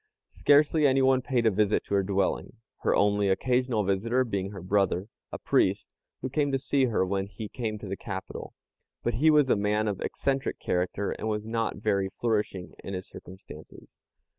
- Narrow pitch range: No, average, 4.6 semitones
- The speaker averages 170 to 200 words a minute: Yes, average, 185 wpm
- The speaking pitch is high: No, low, 105 Hz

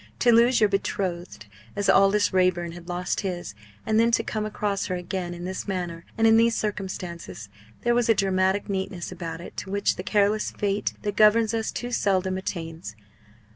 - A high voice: Yes, high, 195 Hz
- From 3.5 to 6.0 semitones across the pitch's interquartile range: No, average, 3.1 semitones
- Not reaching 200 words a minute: Yes, average, 185 wpm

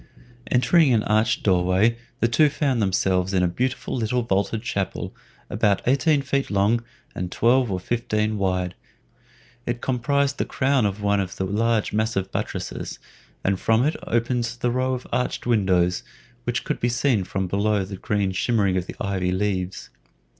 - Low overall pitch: Yes, low, 110 Hz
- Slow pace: No, average, 170 wpm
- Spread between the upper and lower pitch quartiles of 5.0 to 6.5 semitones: No, average, 4.2 semitones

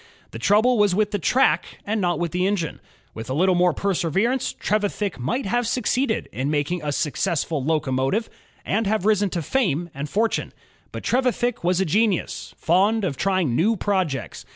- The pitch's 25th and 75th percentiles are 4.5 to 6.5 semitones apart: Yes, average, 5.1 semitones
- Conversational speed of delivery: Yes, average, 175 wpm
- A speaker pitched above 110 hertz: Yes, high, 190 Hz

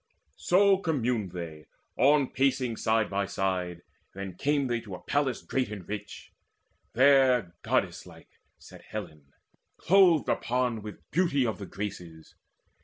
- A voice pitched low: Yes, low, 115 Hz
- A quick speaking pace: No, slow, 135 wpm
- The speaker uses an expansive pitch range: Yes, wide, 6.0 semitones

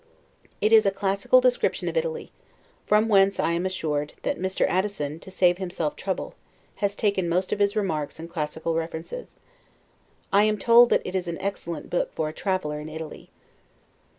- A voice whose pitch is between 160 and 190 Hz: Yes, medium, 185 Hz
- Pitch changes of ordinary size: Yes, average, 3.8 semitones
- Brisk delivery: No, average, 180 wpm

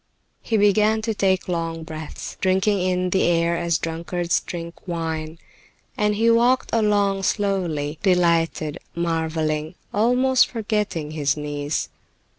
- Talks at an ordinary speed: No, slow, 120 wpm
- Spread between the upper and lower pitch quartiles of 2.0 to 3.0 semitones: No, average, 4.2 semitones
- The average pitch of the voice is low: No, medium, 175 Hz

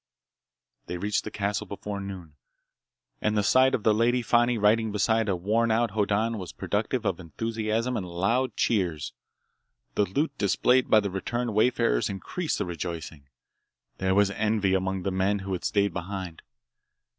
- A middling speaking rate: Yes, average, 160 wpm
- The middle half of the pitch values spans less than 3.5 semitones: Yes, average, 3.1 semitones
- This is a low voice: Yes, low, 105 Hz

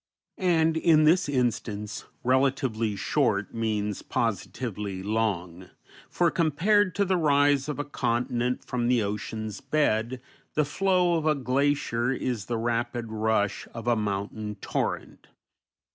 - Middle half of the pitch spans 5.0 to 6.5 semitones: Yes, average, 5.3 semitones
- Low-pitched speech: Yes, low, 120 Hz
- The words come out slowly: Yes, slow, 130 wpm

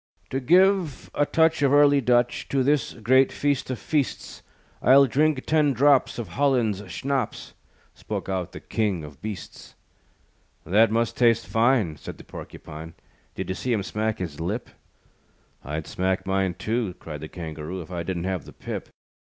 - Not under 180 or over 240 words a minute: No, average, 165 wpm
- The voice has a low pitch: Yes, low, 115 Hz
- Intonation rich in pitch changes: Yes, wide, 6.7 semitones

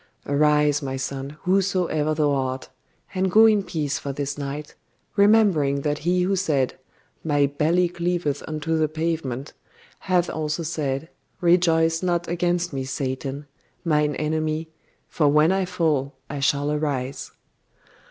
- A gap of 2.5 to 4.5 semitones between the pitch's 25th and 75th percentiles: Yes, average, 3.4 semitones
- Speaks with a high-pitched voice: No, medium, 155 Hz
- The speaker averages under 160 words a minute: Yes, average, 140 wpm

